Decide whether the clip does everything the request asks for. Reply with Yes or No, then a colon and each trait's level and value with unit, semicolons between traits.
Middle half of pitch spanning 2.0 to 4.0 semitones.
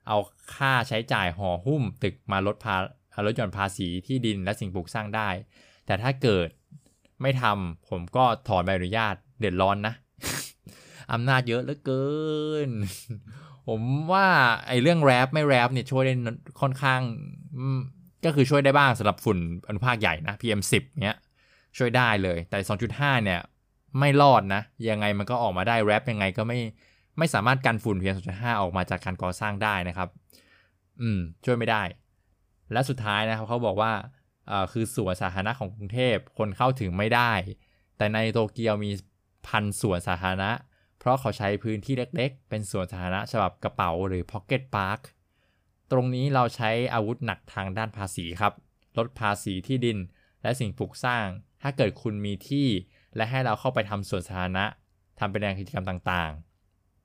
No: average, 4.7 semitones